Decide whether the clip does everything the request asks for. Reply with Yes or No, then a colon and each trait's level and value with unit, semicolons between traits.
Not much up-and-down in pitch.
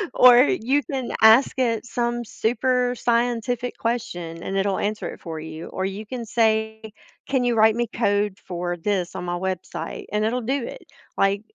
No: average, 3.8 semitones